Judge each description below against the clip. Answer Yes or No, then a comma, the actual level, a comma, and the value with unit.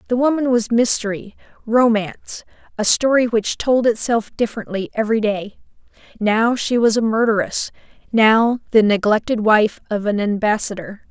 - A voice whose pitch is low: No, high, 220 Hz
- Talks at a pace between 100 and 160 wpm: Yes, slow, 135 wpm